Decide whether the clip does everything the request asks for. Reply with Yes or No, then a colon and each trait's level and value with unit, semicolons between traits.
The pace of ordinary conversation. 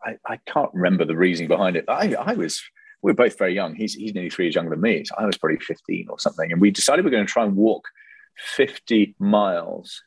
No: fast, 250 wpm